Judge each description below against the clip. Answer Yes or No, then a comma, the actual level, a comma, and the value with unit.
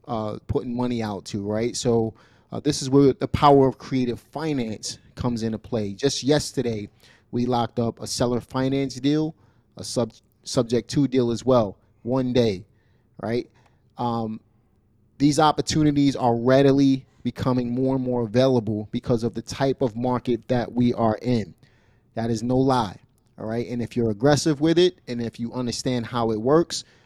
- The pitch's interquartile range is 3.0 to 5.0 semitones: No, narrow, 2.6 semitones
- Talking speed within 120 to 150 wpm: No, average, 170 wpm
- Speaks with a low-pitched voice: Yes, low, 120 Hz